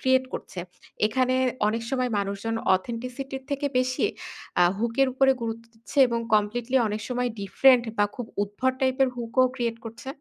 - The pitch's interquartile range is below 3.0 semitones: Yes, narrow, 2.6 semitones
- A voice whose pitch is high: Yes, high, 240 Hz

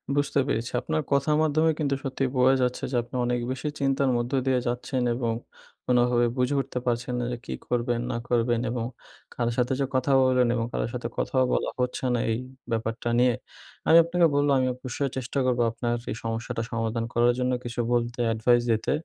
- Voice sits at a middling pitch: No, low, 125 Hz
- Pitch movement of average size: No, narrow, 2.1 semitones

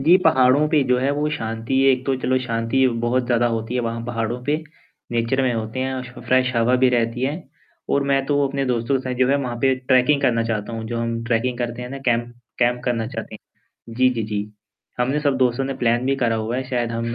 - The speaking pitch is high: No, low, 125 Hz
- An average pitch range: No, narrow, 2.3 semitones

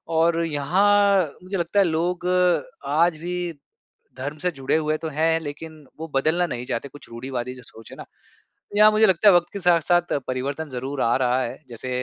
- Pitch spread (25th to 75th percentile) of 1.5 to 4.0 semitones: No, average, 4.7 semitones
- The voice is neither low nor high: Yes, medium, 160 Hz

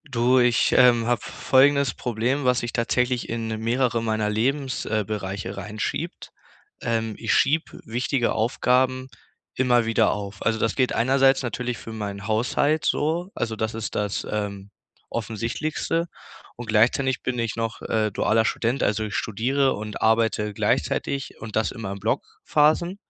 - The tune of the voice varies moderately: Yes, average, 3.1 semitones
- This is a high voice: No, low, 115 Hz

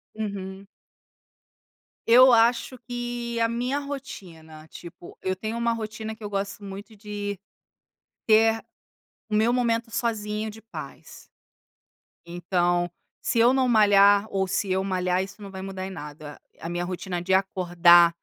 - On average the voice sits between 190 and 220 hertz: Yes, high, 205 Hz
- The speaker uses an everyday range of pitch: Yes, average, 3.7 semitones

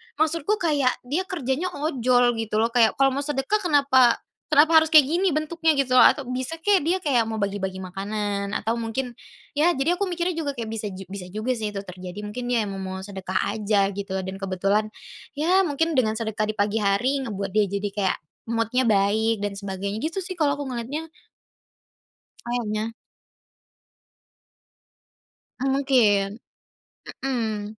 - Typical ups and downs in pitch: No, wide, 6.0 semitones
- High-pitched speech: Yes, high, 235 Hz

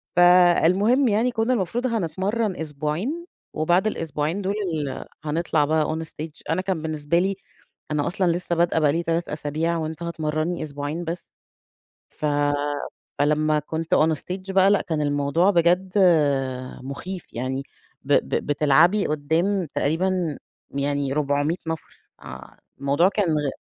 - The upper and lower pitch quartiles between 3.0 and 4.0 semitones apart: Yes, average, 3.7 semitones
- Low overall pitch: No, medium, 165 Hz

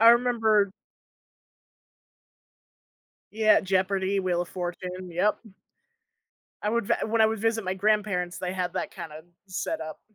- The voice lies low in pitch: No, high, 195 Hz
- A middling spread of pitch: Yes, average, 3.1 semitones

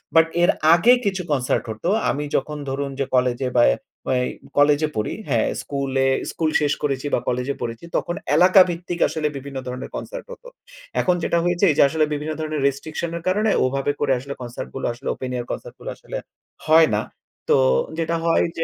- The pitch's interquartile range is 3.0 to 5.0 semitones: Yes, average, 4.0 semitones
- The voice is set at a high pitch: No, medium, 145 Hz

